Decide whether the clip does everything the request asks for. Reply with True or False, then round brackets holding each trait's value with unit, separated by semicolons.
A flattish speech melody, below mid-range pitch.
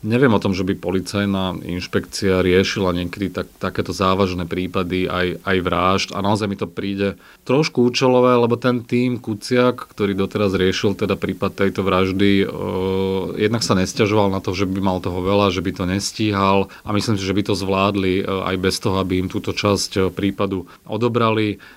True (1.9 semitones; 95 Hz)